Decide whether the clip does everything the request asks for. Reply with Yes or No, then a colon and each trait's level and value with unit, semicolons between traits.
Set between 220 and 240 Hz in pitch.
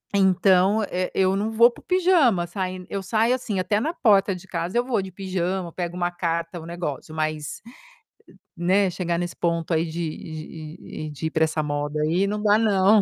No: medium, 185 Hz